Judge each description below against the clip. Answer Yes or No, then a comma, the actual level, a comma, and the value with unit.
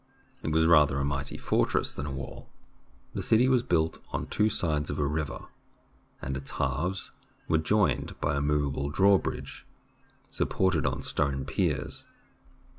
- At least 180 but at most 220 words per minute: No, average, 155 wpm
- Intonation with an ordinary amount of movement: Yes, average, 3.3 semitones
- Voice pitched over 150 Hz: No, very low, 75 Hz